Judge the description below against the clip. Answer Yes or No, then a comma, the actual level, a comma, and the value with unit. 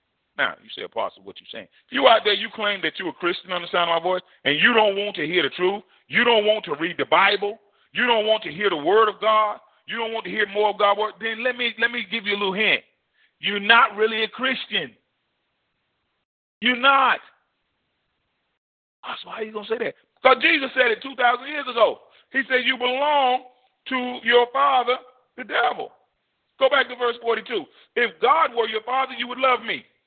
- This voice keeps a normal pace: No, fast, 220 wpm